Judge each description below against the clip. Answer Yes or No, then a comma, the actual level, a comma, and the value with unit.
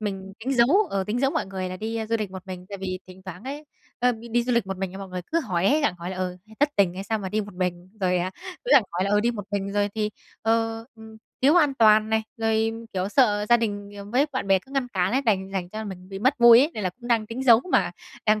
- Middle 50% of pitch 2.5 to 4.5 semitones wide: Yes, average, 3.9 semitones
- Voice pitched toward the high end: Yes, high, 210 Hz